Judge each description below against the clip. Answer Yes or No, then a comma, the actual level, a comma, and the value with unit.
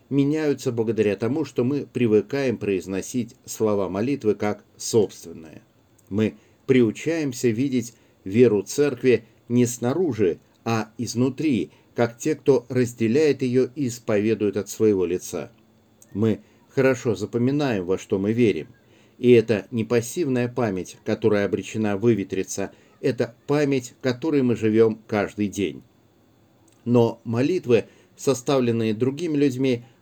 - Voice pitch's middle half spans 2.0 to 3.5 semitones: Yes, average, 2.9 semitones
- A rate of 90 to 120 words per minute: Yes, average, 115 wpm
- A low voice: Yes, low, 115 Hz